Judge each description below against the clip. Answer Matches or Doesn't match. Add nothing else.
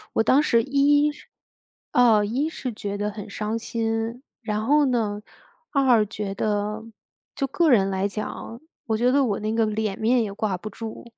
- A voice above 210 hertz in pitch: Matches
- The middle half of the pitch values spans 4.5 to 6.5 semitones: Doesn't match